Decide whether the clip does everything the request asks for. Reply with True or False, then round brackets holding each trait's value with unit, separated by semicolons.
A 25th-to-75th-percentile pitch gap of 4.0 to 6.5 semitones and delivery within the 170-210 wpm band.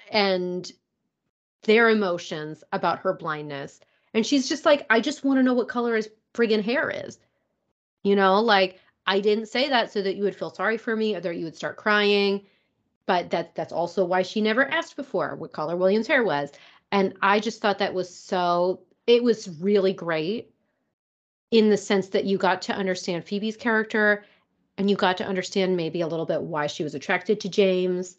False (3.3 semitones; 195 wpm)